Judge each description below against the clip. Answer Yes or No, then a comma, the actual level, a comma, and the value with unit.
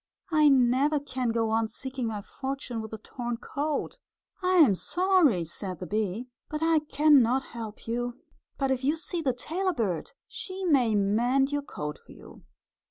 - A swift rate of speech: No, average, 175 wpm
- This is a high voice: Yes, very high, 255 Hz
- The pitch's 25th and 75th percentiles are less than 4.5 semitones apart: No, average, 5.0 semitones